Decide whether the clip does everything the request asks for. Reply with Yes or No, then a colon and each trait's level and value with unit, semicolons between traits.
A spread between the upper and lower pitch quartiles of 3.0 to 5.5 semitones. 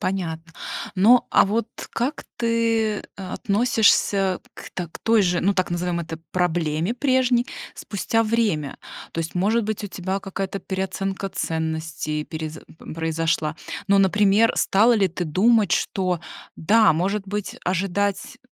Yes: average, 4.1 semitones